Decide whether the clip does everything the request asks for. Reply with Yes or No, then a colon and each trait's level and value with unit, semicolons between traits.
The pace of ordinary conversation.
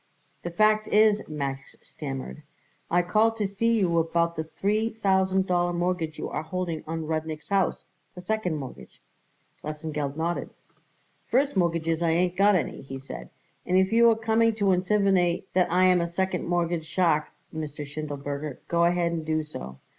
Yes: average, 170 wpm